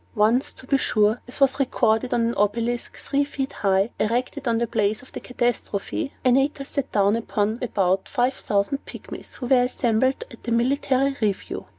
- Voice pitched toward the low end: No, high, 240 Hz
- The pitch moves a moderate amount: Yes, average, 3.5 semitones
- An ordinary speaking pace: Yes, average, 180 wpm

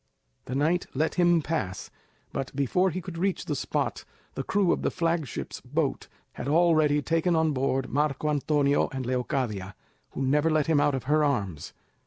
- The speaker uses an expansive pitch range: No, average, 3.6 semitones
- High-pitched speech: No, medium, 150 Hz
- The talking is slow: No, average, 175 wpm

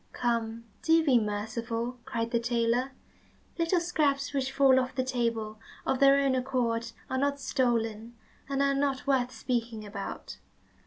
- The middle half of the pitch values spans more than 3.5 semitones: No, average, 3.0 semitones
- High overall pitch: Yes, very high, 250 Hz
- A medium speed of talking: Yes, average, 150 wpm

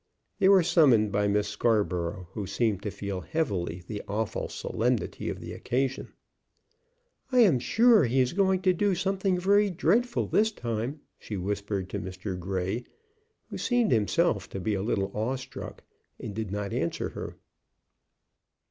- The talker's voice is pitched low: Yes, low, 115 Hz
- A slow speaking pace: No, average, 155 wpm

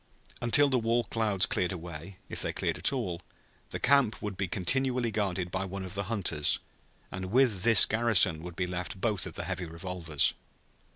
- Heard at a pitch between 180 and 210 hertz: No, very low, 95 Hz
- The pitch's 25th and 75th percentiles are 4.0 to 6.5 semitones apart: Yes, average, 4.3 semitones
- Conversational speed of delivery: Yes, average, 185 wpm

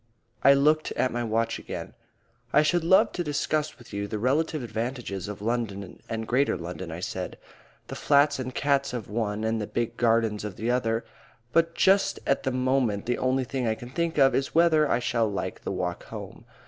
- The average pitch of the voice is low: Yes, low, 125 Hz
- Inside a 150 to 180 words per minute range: No, average, 200 wpm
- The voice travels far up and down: No, average, 4.2 semitones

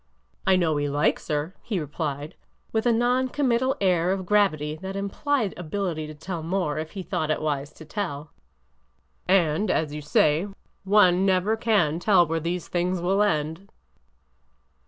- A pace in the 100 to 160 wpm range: No, average, 170 wpm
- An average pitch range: Yes, average, 4.5 semitones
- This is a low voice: No, medium, 180 Hz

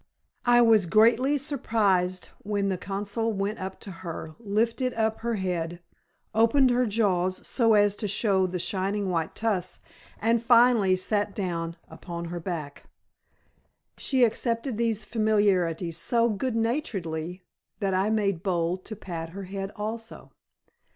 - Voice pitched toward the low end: No, high, 205 Hz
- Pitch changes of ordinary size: Yes, average, 3.8 semitones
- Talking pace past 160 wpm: No, average, 140 wpm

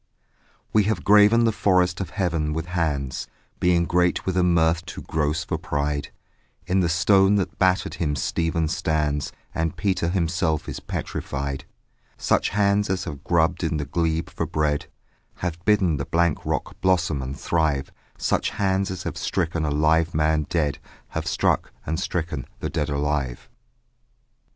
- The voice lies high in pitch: No, very low, 85 Hz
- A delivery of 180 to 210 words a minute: No, average, 160 wpm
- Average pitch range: Yes, average, 3.4 semitones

